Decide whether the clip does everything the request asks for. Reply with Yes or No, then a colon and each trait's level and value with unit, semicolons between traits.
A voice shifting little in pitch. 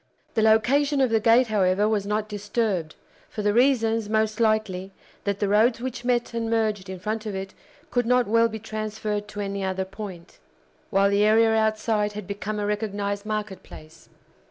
Yes: narrow, 1.8 semitones